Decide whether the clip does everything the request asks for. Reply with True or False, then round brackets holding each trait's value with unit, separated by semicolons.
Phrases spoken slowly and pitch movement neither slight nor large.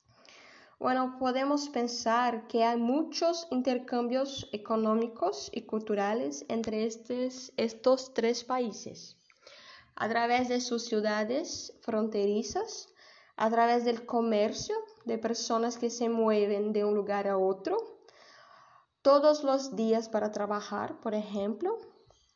True (115 wpm; 3.6 semitones)